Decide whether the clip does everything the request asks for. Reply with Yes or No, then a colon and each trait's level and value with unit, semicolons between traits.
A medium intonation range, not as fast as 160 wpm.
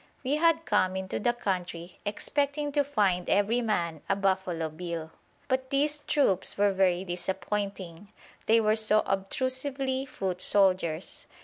No: wide, 6.2 semitones; slow, 135 wpm